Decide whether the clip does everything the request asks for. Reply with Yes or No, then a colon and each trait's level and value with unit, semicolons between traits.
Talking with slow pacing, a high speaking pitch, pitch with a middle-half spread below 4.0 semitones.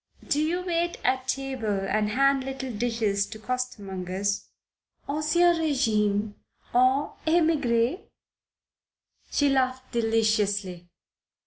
No: slow, 100 wpm; very high, 250 Hz; average, 5.0 semitones